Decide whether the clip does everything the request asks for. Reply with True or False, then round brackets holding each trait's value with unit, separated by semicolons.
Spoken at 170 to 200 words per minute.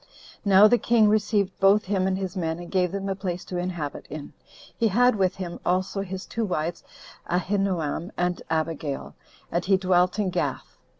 True (180 wpm)